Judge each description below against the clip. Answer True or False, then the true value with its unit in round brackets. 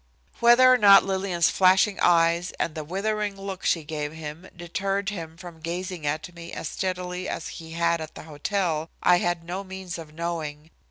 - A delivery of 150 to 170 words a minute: False (180 wpm)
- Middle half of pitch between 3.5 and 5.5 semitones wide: False (2.9 semitones)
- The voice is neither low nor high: True (175 Hz)